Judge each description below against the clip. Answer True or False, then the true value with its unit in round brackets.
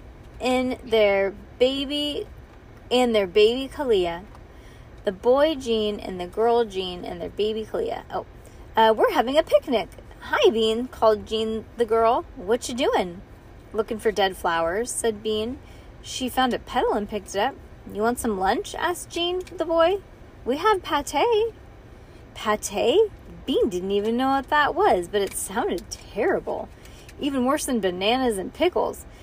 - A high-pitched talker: True (235 Hz)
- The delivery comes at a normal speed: True (155 wpm)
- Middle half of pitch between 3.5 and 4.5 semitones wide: False (5.4 semitones)